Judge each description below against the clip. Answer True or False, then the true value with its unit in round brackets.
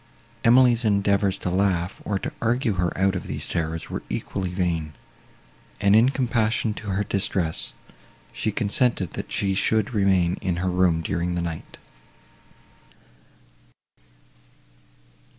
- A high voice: False (95 Hz)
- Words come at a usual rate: False (130 wpm)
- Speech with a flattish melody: False (3.5 semitones)